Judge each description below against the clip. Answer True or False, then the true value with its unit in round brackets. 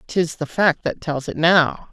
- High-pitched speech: False (160 Hz)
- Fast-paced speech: True (220 wpm)